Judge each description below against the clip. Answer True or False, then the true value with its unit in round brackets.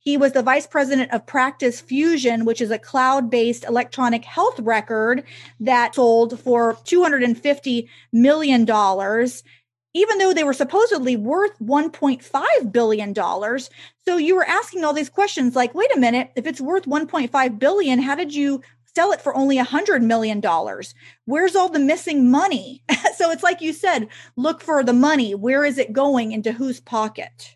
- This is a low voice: False (265 Hz)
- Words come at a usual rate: True (165 wpm)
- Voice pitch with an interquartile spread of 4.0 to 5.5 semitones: True (4.4 semitones)